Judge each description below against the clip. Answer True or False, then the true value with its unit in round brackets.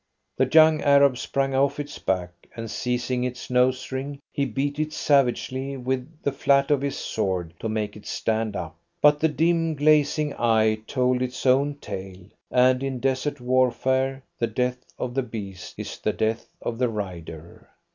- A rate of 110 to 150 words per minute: False (170 wpm)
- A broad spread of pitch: False (3.9 semitones)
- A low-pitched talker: True (130 Hz)